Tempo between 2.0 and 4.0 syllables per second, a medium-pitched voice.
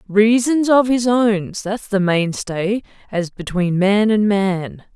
No: 3.5 syllables/s; high, 205 Hz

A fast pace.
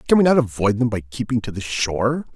Yes: fast, 255 wpm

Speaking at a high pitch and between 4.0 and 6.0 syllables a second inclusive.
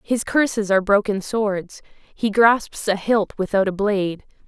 Yes: high, 205 Hz; 4.2 syllables/s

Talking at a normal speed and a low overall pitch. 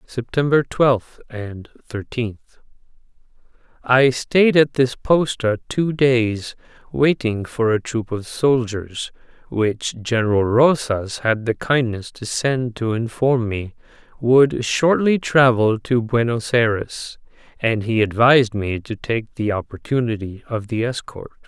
No: slow, 125 wpm; low, 120 Hz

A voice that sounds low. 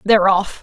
No: high, 195 Hz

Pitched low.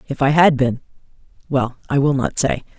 Yes: low, 130 Hz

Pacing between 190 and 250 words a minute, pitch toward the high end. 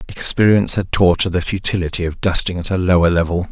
No: fast, 205 wpm; very low, 90 Hz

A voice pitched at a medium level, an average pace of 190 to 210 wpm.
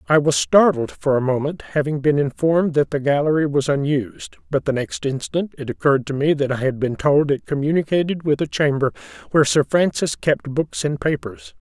Yes: medium, 145 Hz; average, 200 wpm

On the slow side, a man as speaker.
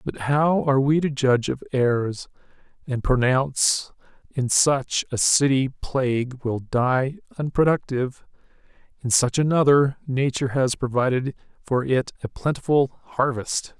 Yes: slow, 120 wpm; male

